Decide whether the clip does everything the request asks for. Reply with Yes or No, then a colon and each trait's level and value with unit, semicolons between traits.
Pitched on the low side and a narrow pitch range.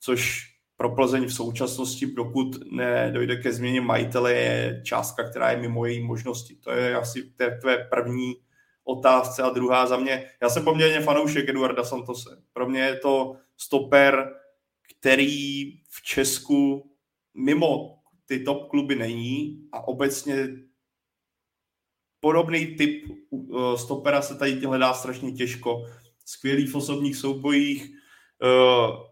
Yes: low, 130 Hz; narrow, 2.2 semitones